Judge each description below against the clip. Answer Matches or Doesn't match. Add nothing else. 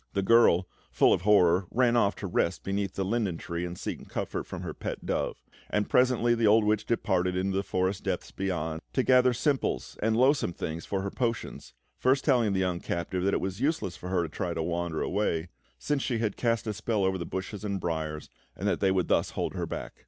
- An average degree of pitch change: Matches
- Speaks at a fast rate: Matches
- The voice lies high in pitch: Doesn't match